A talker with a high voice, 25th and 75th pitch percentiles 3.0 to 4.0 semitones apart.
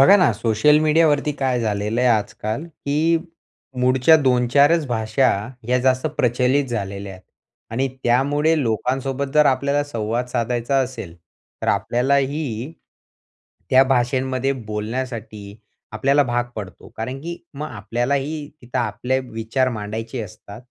No: low, 125 Hz; average, 3.7 semitones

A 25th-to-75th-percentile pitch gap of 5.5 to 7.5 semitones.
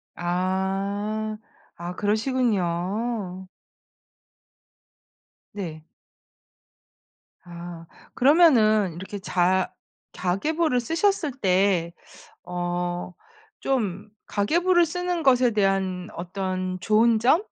No: average, 5.1 semitones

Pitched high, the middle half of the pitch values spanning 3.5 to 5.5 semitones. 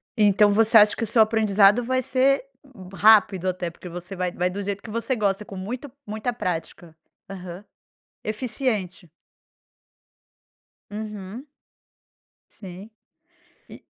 No: high, 205 Hz; average, 3.1 semitones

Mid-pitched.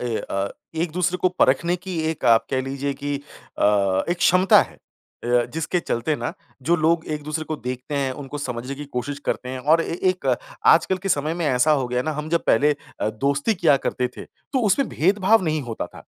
Yes: medium, 145 Hz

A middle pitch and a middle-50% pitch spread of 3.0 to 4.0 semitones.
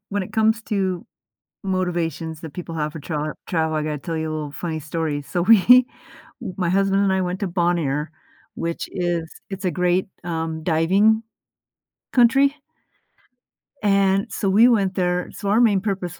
Yes: medium, 180 Hz; average, 3.4 semitones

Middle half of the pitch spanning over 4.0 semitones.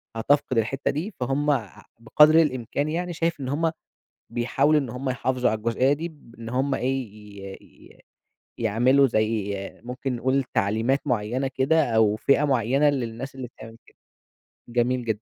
No: average, 3.7 semitones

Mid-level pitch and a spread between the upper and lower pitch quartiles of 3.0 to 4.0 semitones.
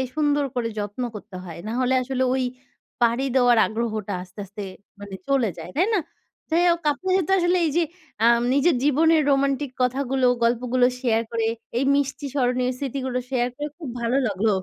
No: very high, 255 Hz; average, 3.4 semitones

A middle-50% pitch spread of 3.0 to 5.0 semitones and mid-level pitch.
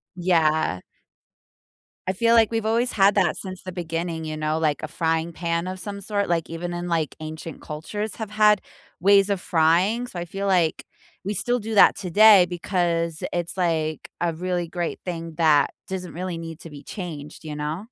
Yes: average, 3.4 semitones; medium, 175 Hz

